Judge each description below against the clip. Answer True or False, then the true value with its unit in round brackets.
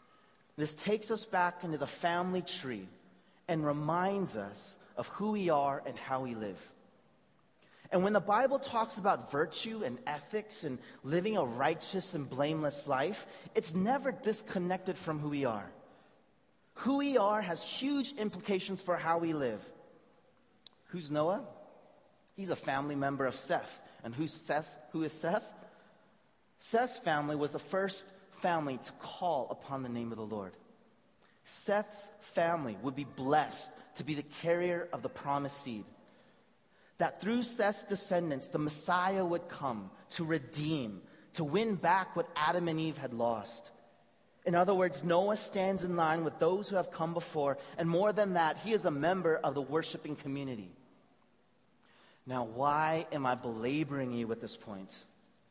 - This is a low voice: False (165 Hz)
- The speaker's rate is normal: True (160 wpm)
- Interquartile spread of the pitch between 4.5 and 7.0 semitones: True (5.5 semitones)